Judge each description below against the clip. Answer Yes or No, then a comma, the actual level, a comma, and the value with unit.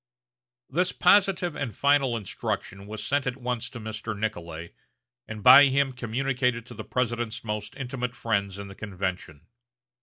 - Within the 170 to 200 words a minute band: No, average, 150 wpm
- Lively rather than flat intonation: No, average, 4.0 semitones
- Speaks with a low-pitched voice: Yes, low, 115 Hz